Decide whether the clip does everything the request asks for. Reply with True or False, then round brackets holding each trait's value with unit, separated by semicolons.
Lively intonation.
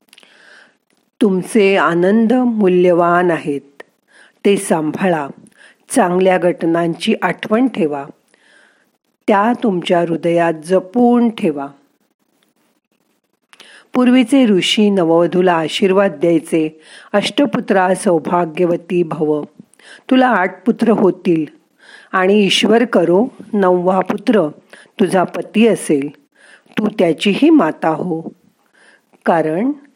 False (4.9 semitones)